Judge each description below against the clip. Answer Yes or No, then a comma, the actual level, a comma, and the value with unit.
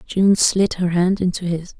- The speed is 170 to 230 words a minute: Yes, average, 200 wpm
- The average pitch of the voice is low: No, medium, 180 Hz